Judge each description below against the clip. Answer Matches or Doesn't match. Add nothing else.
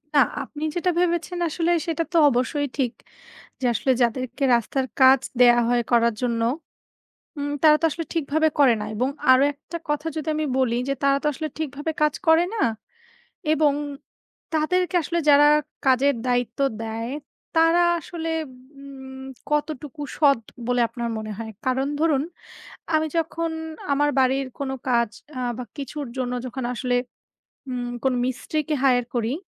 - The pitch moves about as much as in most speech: Matches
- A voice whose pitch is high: Matches